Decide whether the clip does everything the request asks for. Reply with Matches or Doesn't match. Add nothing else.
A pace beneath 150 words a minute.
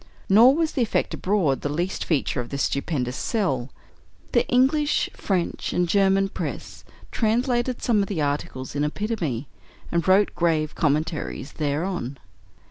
Matches